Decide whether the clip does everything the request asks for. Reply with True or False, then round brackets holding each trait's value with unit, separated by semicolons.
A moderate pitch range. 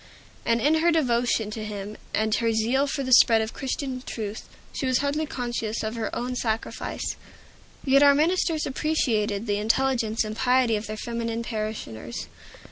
True (3.6 semitones)